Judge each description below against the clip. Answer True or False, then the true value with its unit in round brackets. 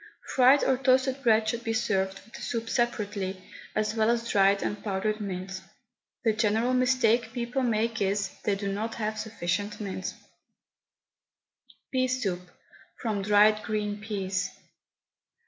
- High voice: True (215 Hz)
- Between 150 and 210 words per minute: False (140 wpm)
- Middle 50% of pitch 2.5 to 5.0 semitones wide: True (2.9 semitones)